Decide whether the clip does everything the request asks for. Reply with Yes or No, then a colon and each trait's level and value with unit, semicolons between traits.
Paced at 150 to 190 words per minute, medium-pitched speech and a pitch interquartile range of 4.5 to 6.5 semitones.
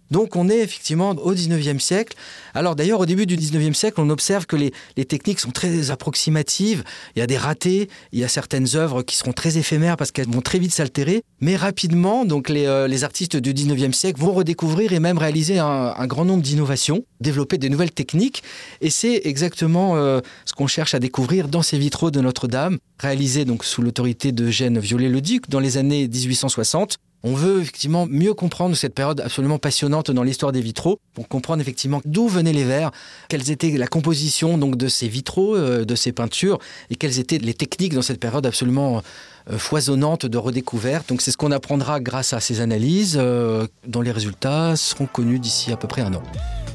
No: average, 200 wpm; medium, 145 Hz; average, 4.8 semitones